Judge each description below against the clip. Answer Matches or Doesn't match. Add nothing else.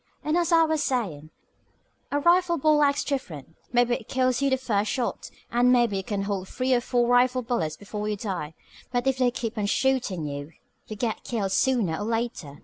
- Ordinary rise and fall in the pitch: Matches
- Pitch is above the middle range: Matches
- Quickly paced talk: Matches